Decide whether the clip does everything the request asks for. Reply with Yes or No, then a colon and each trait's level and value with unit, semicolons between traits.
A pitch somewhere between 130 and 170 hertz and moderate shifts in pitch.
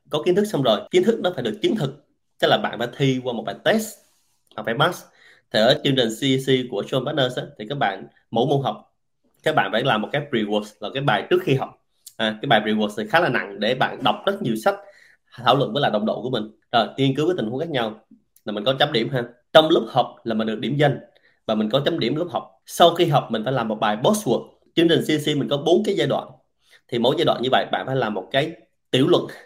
No: low, 135 Hz; wide, 6.1 semitones